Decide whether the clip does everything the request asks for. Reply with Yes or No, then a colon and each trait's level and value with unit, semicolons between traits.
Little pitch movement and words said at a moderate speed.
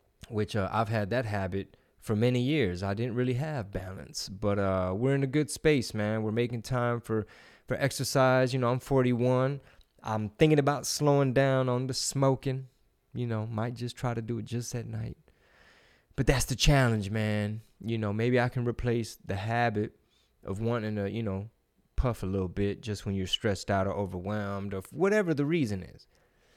No: average, 3.9 semitones; average, 190 wpm